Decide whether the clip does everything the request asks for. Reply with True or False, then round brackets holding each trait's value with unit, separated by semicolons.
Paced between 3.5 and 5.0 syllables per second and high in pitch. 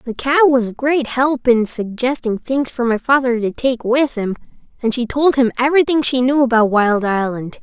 True (4.9 syllables/s; 250 Hz)